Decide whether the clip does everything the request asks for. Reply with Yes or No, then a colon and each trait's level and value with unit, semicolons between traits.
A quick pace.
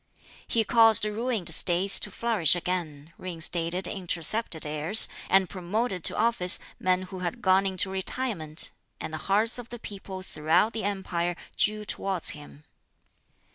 No: average, 140 wpm